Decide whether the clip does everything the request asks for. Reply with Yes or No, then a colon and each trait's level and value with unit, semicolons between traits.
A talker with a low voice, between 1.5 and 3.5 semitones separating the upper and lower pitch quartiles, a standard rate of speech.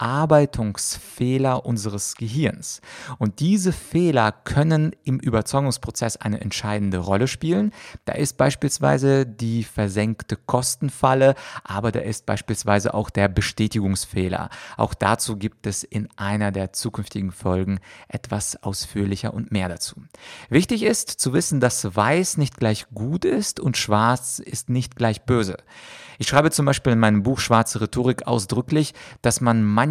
No: low, 115 Hz; average, 4.1 semitones; average, 140 wpm